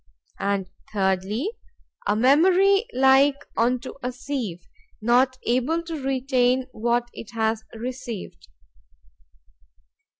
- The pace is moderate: No, slow, 95 wpm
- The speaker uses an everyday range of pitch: Yes, average, 3.5 semitones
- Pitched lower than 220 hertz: No, very high, 250 Hz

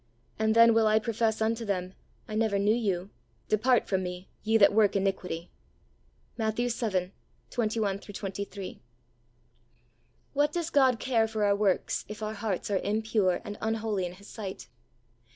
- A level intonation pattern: Yes, narrow, 2.3 semitones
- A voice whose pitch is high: Yes, high, 215 Hz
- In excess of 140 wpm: Yes, average, 150 wpm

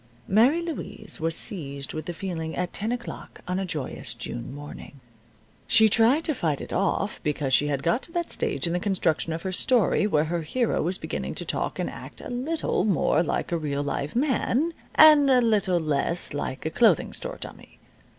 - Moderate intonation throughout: No, wide, 7.6 semitones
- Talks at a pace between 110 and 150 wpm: No, average, 200 wpm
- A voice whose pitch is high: No, medium, 180 Hz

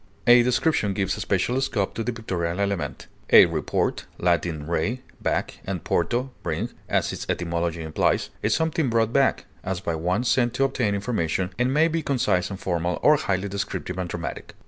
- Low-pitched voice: Yes, low, 100 Hz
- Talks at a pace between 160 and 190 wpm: Yes, average, 175 wpm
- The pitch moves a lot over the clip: Yes, wide, 6.0 semitones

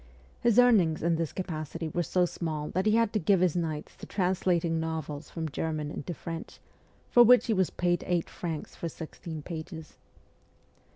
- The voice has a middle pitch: Yes, medium, 170 Hz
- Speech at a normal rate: Yes, average, 175 wpm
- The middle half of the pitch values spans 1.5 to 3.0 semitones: Yes, narrow, 2.5 semitones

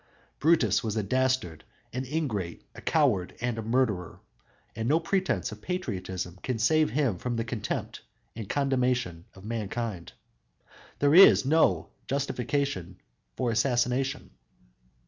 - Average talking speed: No, slow, 125 wpm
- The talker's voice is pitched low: Yes, low, 120 Hz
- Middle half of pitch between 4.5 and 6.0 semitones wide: Yes, average, 5.2 semitones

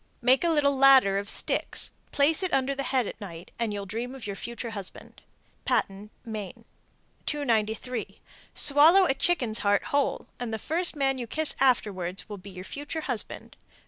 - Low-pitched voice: No, high, 245 Hz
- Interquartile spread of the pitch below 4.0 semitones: No, wide, 5.4 semitones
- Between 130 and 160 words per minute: No, average, 175 wpm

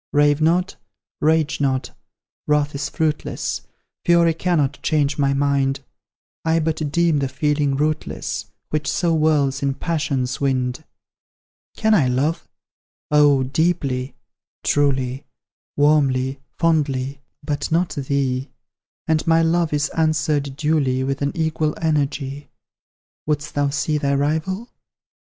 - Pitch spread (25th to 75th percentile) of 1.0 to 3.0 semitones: Yes, narrow, 2.4 semitones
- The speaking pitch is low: No, medium, 145 Hz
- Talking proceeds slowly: Yes, slow, 120 wpm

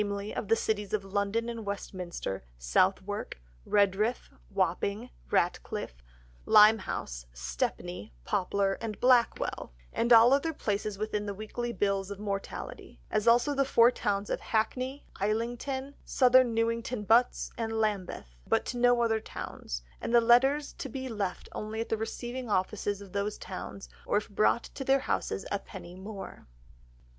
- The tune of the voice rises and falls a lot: No, average, 3.2 semitones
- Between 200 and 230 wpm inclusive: No, average, 150 wpm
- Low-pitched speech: No, high, 215 Hz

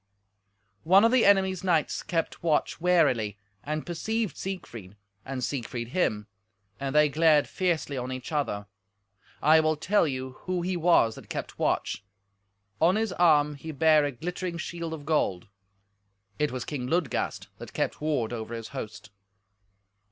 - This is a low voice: No, medium, 155 Hz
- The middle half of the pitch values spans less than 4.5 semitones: No, average, 5.2 semitones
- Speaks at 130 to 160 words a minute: Yes, average, 150 wpm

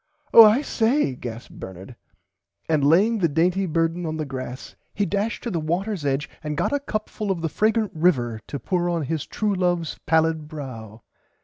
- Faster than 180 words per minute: Yes, average, 190 wpm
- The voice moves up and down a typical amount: No, wide, 5.8 semitones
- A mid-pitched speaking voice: Yes, medium, 165 Hz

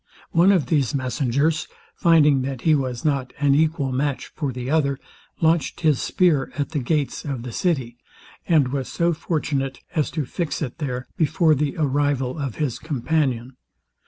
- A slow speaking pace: No, average, 165 wpm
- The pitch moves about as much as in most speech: Yes, average, 3.2 semitones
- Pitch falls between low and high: Yes, medium, 145 Hz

